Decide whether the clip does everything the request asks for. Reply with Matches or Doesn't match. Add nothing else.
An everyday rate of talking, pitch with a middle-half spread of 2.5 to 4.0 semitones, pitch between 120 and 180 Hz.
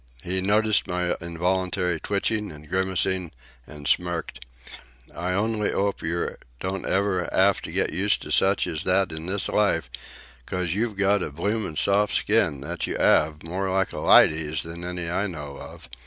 Doesn't match